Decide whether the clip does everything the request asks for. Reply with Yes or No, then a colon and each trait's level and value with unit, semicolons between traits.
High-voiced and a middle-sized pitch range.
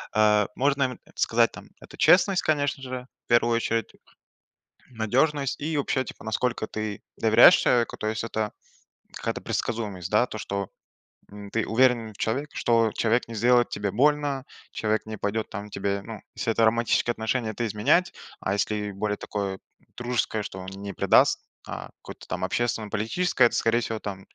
No: low, 115 Hz; average, 3.1 semitones